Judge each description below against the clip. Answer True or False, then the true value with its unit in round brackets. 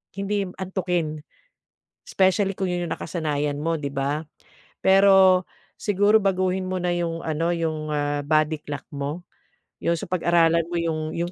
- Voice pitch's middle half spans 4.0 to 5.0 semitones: False (3.3 semitones)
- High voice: False (170 Hz)